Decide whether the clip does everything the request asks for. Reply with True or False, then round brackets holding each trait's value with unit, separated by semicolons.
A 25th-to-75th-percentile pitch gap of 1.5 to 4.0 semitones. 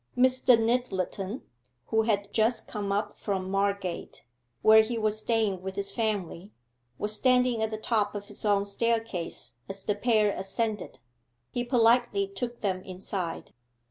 True (2.6 semitones)